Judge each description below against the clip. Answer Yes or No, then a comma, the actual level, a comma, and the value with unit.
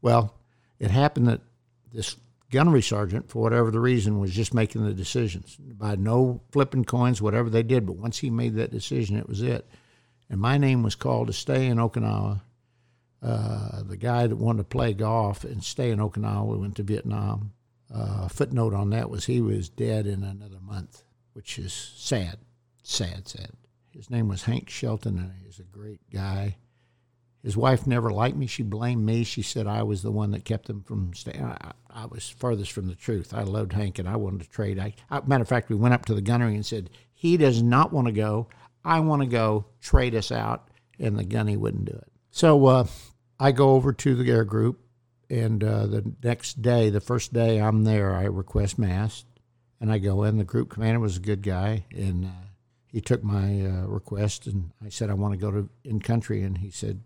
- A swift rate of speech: Yes, fast, 215 wpm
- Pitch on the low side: Yes, low, 110 Hz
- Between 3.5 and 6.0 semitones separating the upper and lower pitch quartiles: No, average, 2.8 semitones